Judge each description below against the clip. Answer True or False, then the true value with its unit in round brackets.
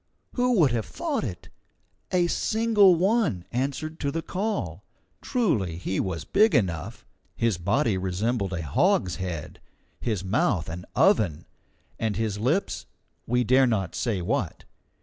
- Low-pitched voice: True (115 Hz)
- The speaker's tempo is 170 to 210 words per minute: False (135 wpm)